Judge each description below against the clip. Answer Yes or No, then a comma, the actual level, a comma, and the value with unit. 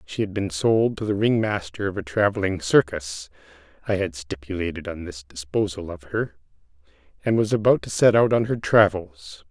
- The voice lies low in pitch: Yes, low, 105 Hz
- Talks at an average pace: Yes, average, 185 wpm